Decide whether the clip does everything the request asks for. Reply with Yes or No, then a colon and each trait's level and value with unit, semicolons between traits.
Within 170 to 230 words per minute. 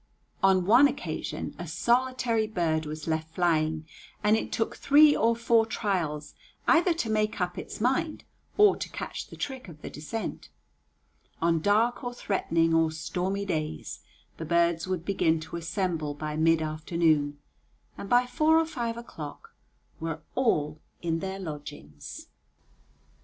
No: average, 145 wpm